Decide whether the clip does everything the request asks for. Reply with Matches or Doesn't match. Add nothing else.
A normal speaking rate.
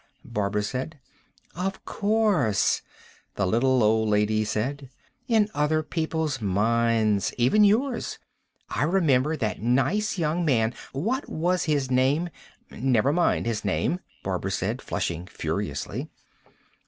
Doesn't match